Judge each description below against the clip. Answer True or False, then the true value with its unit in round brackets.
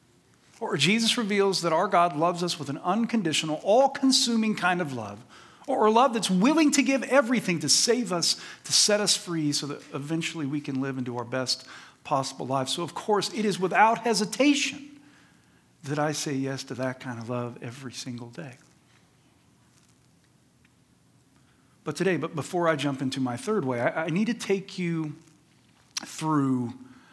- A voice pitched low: False (165 Hz)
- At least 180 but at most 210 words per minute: False (170 wpm)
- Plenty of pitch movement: True (7.7 semitones)